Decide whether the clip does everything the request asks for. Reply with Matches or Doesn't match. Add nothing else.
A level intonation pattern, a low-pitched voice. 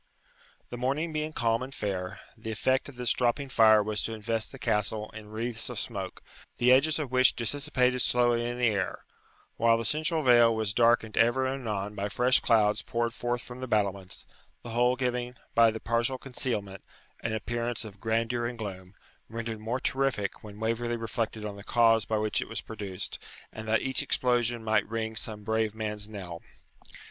Matches